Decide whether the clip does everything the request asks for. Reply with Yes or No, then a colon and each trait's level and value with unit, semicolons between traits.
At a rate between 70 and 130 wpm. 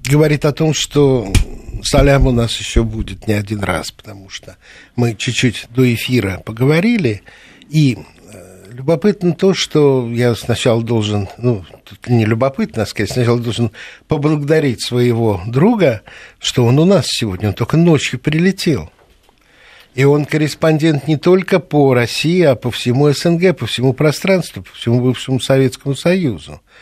No: average, 145 wpm